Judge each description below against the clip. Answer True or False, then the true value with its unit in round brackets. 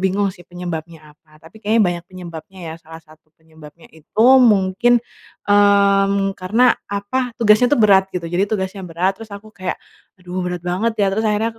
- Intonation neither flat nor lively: True (3.5 semitones)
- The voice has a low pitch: False (190 Hz)